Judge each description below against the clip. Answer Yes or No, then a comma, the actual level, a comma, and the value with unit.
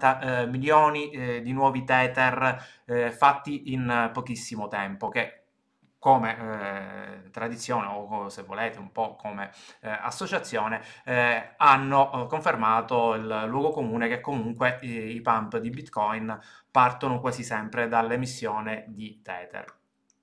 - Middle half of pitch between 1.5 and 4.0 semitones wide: Yes, average, 3.0 semitones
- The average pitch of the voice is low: Yes, low, 120 Hz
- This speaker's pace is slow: Yes, slow, 105 wpm